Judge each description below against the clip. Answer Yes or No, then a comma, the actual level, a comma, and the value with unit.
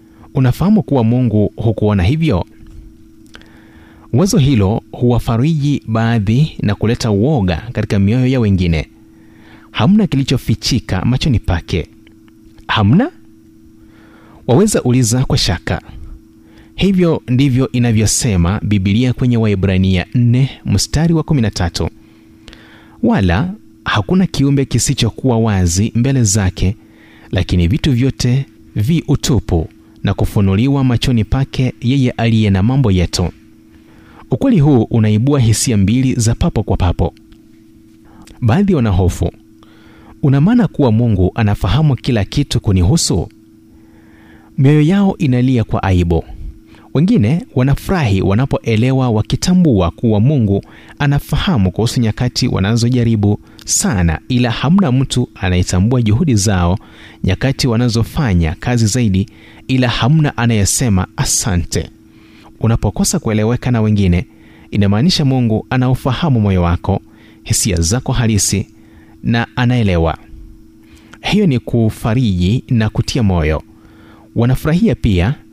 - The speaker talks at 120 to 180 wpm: No, slow, 100 wpm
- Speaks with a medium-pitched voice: No, low, 110 Hz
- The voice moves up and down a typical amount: Yes, average, 4.1 semitones